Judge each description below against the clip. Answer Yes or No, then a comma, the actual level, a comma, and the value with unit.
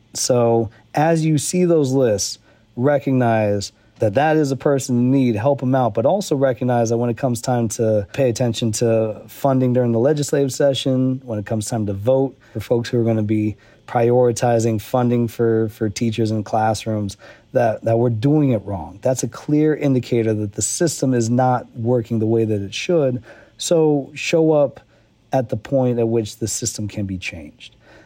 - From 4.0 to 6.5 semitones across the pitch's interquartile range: No, average, 3.2 semitones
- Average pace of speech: Yes, average, 190 wpm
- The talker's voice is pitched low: Yes, low, 120 Hz